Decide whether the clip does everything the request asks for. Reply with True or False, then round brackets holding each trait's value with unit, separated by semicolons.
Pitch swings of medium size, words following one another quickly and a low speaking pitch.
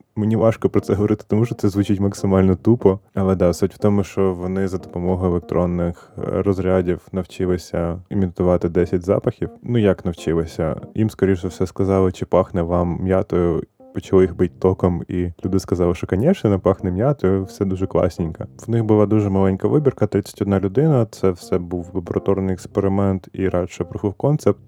False (2.3 semitones; 170 wpm; 95 Hz)